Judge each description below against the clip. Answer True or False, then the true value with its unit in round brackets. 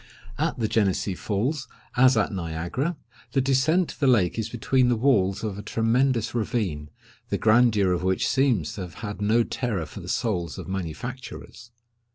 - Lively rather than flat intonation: False (4.9 semitones)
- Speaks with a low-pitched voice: True (110 Hz)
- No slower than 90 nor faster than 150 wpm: False (175 wpm)